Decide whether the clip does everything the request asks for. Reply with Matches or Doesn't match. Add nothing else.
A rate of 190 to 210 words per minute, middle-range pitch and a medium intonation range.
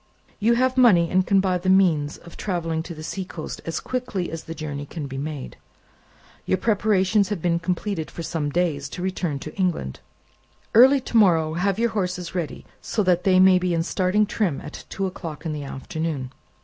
Matches